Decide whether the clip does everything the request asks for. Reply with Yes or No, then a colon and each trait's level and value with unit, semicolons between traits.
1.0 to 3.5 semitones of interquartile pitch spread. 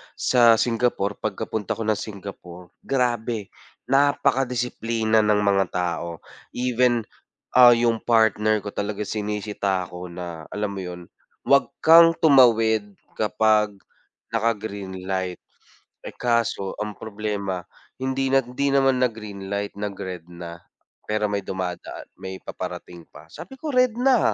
No: average, 3.9 semitones